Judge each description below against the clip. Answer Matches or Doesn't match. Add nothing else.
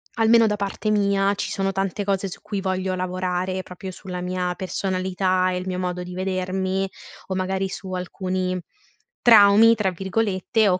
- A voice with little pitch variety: Matches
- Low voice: Doesn't match